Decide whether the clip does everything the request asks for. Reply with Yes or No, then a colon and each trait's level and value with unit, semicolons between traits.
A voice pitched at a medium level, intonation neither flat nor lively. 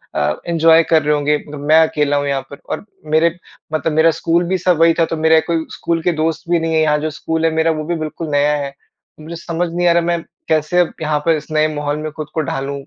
No: medium, 160 Hz; narrow, 1.8 semitones